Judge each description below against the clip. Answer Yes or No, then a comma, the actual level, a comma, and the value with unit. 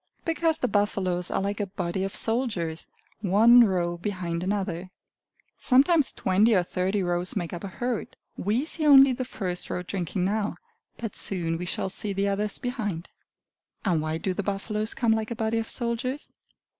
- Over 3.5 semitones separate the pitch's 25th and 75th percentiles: Yes, average, 4.3 semitones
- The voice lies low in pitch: No, high, 200 Hz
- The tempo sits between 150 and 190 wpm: Yes, average, 175 wpm